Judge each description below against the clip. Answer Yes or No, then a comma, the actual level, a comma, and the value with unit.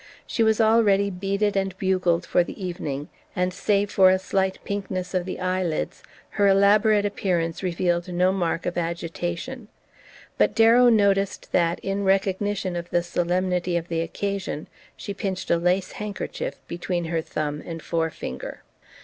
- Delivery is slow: No, average, 155 wpm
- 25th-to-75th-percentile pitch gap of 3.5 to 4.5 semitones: No, narrow, 2.5 semitones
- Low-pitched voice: No, medium, 185 Hz